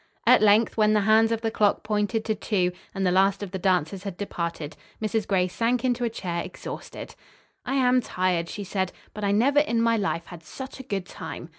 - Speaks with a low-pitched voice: No, high, 205 Hz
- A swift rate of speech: Yes, fast, 215 wpm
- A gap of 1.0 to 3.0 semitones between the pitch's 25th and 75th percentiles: No, average, 3.5 semitones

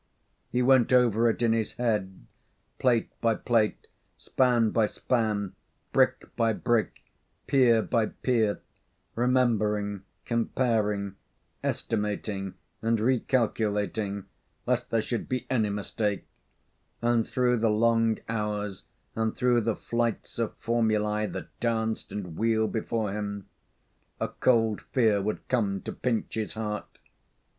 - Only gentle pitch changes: Yes, narrow, 2.1 semitones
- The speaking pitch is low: Yes, low, 110 Hz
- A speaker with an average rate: No, slow, 120 wpm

